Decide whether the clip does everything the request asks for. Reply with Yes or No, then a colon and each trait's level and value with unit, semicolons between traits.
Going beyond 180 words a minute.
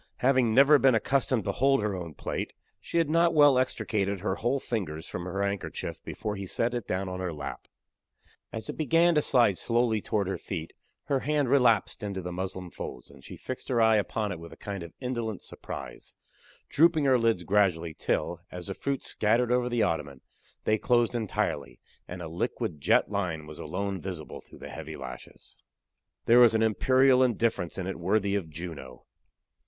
Yes: average, 190 wpm